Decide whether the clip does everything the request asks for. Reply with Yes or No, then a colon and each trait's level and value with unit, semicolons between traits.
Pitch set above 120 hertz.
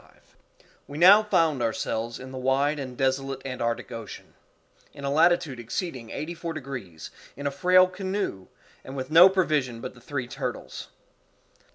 Yes: medium, 140 Hz